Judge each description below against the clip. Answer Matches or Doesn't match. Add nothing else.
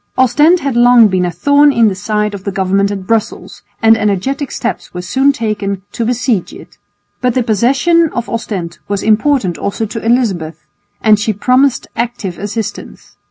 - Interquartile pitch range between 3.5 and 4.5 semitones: Matches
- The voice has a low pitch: Doesn't match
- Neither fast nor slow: Matches